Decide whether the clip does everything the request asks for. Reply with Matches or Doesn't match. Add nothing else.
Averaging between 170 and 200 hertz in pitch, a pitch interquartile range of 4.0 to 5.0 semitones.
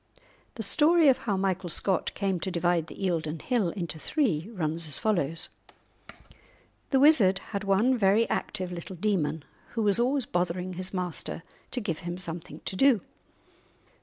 Matches